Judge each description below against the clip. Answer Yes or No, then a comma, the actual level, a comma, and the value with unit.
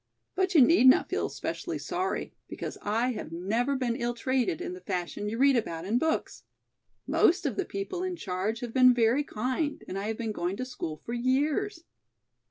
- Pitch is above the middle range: Yes, high, 240 Hz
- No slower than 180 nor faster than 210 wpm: Yes, average, 195 wpm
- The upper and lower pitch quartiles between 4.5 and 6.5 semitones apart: Yes, average, 5.3 semitones